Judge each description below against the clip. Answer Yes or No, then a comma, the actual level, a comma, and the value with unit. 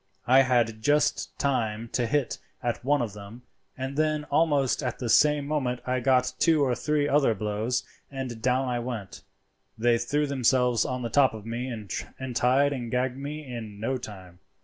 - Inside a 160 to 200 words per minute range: Yes, average, 180 wpm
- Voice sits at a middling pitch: No, low, 125 Hz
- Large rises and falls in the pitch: No, average, 3.2 semitones